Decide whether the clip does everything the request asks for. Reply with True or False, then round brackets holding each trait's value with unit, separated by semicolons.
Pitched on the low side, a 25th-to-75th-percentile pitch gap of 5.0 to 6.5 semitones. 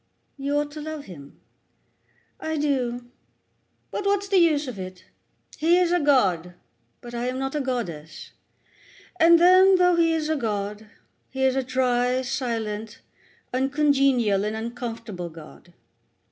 False (255 Hz; 5.6 semitones)